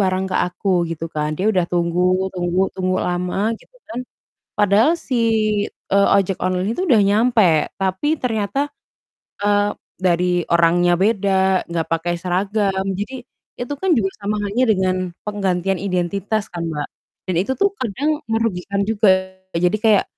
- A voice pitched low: No, high, 195 Hz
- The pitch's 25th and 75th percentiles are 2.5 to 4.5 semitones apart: Yes, average, 3.1 semitones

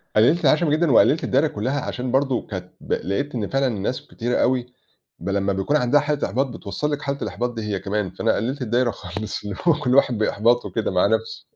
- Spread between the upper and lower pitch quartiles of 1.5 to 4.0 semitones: No, average, 4.8 semitones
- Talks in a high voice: No, low, 125 Hz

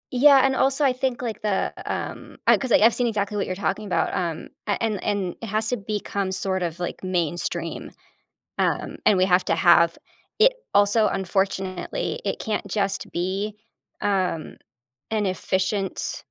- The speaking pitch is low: No, high, 200 Hz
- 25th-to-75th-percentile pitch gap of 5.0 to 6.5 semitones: No, average, 2.9 semitones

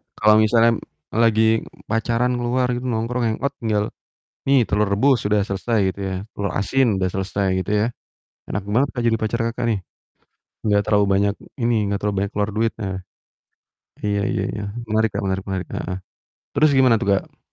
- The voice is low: Yes, low, 110 Hz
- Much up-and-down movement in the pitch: No, average, 2.7 semitones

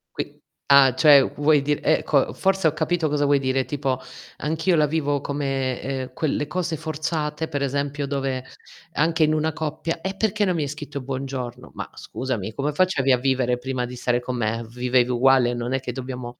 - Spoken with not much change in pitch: No, average, 3.3 semitones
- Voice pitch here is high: No, medium, 140 Hz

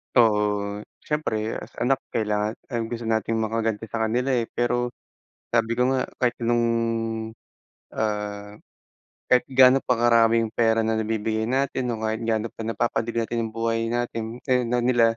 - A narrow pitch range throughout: Yes, narrow, 1.6 semitones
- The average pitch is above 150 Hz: No, low, 115 Hz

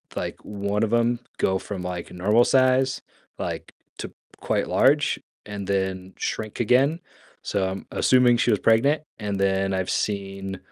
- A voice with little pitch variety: No, average, 3.8 semitones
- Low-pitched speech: Yes, low, 105 Hz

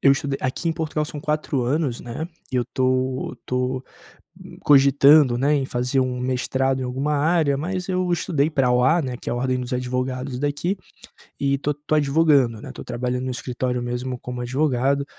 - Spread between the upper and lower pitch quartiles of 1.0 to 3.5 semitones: Yes, average, 2.8 semitones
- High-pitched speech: No, low, 135 Hz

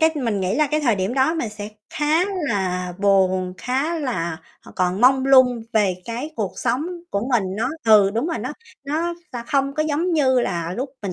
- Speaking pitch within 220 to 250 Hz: Yes, high, 240 Hz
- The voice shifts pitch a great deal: Yes, wide, 6.1 semitones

